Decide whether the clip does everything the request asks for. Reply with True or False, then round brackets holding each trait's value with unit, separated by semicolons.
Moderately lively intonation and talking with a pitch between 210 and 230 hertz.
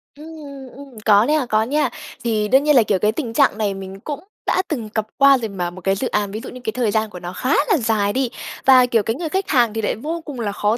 True (4.6 semitones; 225 Hz)